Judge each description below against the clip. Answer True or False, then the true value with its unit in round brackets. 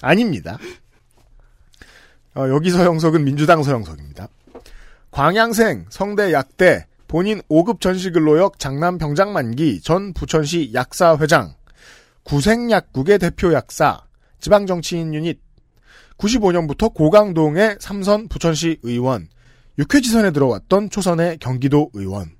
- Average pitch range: False (5.7 semitones)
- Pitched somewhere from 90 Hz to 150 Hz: False (165 Hz)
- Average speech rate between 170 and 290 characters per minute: True (250 characters per minute)